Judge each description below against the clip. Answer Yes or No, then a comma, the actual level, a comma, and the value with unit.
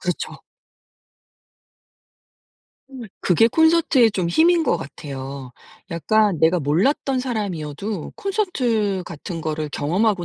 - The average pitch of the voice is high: Yes, high, 195 Hz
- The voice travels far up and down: Yes, wide, 7.8 semitones